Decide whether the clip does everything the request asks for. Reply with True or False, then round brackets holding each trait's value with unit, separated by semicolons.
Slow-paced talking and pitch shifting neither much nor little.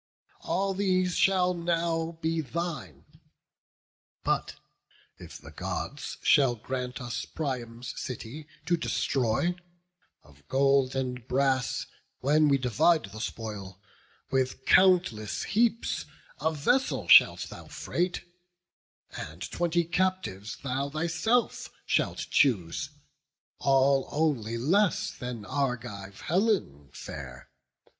False (105 wpm; 6.4 semitones)